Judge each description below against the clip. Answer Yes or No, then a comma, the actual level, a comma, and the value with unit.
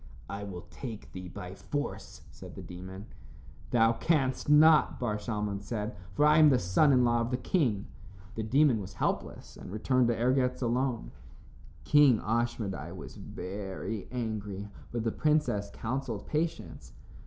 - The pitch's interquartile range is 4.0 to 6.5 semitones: Yes, average, 4.5 semitones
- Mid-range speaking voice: No, low, 115 Hz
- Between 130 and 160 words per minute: Yes, average, 155 wpm